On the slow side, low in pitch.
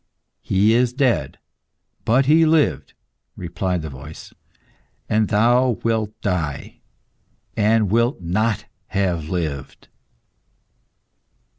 Yes: slow, 95 wpm; low, 105 Hz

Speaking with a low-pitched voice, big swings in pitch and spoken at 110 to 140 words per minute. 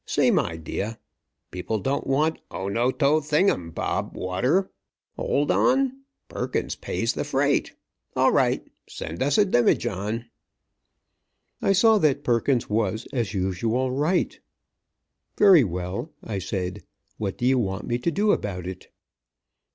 Yes: low, 120 Hz; wide, 8.0 semitones; slow, 135 wpm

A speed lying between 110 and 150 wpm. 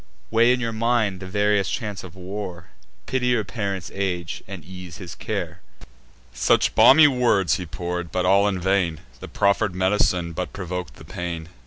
No: average, 170 wpm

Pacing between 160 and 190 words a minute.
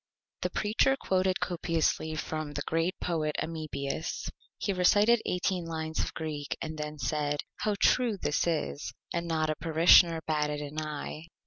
No: average, 150 wpm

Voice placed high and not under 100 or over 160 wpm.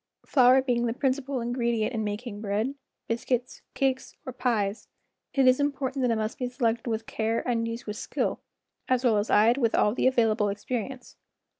No: high, 240 Hz; average, 180 wpm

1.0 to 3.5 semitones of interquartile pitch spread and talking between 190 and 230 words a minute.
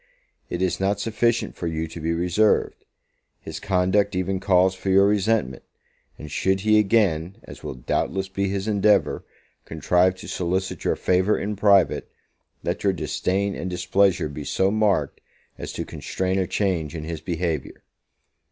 No: average, 2.8 semitones; average, 160 wpm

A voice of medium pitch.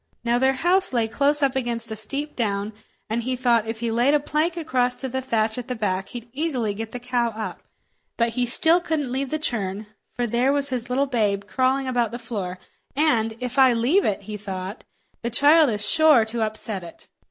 No: high, 240 Hz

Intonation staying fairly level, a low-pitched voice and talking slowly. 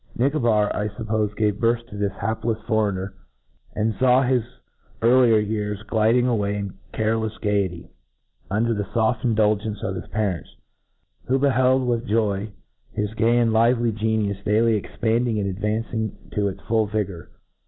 No: narrow, 2.1 semitones; low, 110 Hz; average, 150 wpm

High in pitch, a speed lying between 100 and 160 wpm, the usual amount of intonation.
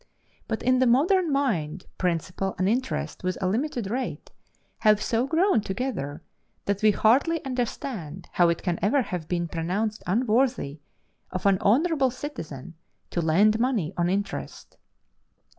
No: high, 210 Hz; average, 140 wpm; wide, 6.3 semitones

